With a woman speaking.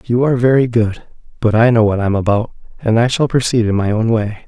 No: male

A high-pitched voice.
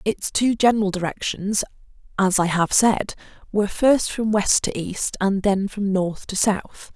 Yes: high, 200 Hz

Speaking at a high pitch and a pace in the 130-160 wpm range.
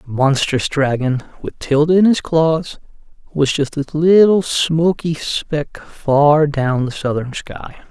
No: medium, 150 Hz; average, 145 wpm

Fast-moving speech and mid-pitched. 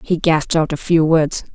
Yes: fast, 235 wpm; medium, 160 Hz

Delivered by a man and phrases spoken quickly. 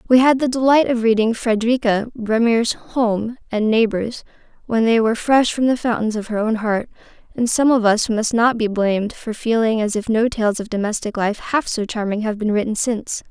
No: female; fast, 210 wpm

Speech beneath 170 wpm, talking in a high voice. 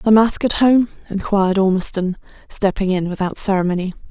Yes: average, 145 wpm; high, 195 Hz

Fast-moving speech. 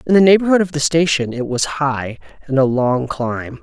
Yes: fast, 215 wpm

